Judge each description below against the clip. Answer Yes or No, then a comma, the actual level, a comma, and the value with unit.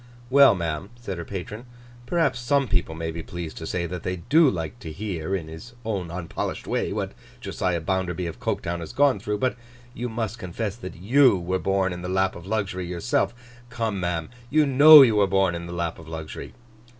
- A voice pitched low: Yes, very low, 95 Hz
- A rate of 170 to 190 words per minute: No, fast, 205 wpm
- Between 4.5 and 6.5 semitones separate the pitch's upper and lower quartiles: Yes, average, 5.0 semitones